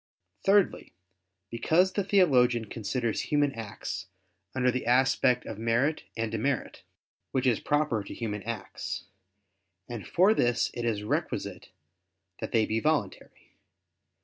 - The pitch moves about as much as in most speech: Yes, average, 4.4 semitones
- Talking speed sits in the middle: No, slow, 125 wpm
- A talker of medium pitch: No, low, 120 Hz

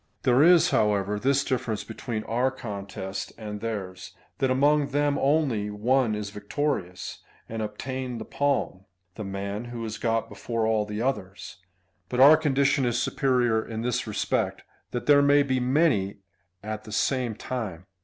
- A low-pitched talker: Yes, low, 115 Hz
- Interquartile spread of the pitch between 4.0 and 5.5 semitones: Yes, average, 4.3 semitones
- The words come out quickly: No, average, 165 wpm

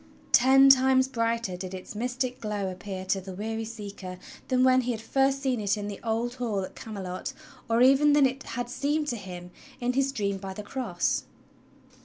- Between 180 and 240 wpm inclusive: Yes, average, 195 wpm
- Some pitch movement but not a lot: Yes, average, 4.6 semitones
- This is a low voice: No, high, 230 Hz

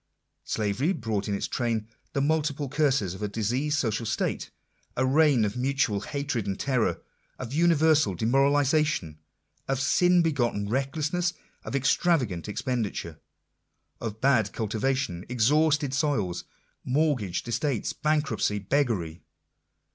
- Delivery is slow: Yes, slow, 115 wpm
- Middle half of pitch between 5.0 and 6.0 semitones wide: Yes, wide, 5.5 semitones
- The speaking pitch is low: Yes, low, 130 Hz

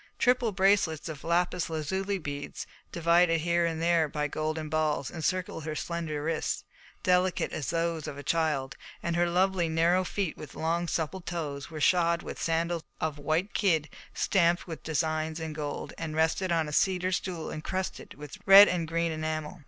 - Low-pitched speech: No, medium, 165 Hz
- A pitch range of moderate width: No, narrow, 2.1 semitones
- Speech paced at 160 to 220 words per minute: Yes, average, 170 wpm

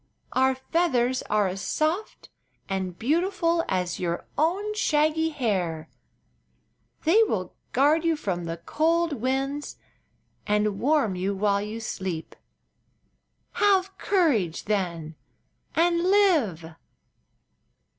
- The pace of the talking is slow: Yes, slow, 105 wpm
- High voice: Yes, very high, 260 Hz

